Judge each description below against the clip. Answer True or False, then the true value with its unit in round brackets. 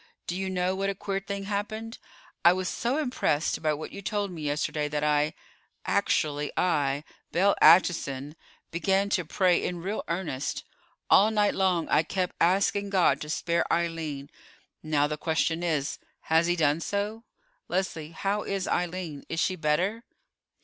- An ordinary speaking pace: True (165 wpm)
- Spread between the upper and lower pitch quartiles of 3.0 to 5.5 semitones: True (4.2 semitones)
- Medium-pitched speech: True (175 Hz)